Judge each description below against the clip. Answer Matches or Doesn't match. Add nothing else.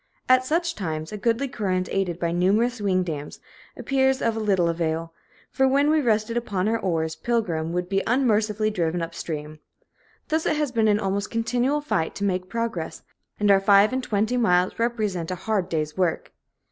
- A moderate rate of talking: Matches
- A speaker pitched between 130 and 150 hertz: Doesn't match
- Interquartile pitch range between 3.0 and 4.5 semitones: Doesn't match